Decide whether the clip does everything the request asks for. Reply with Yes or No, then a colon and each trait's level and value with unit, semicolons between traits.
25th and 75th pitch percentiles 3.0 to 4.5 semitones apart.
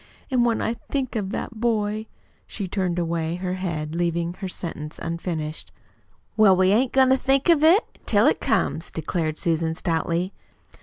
No: average, 5.1 semitones